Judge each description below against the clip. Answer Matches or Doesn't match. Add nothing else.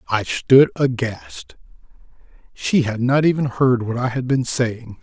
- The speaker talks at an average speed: Matches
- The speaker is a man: Matches